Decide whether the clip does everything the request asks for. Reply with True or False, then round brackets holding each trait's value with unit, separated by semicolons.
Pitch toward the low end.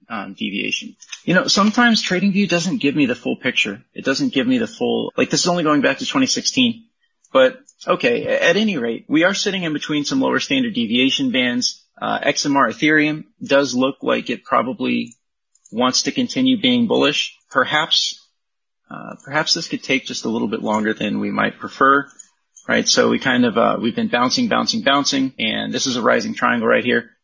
False (235 Hz)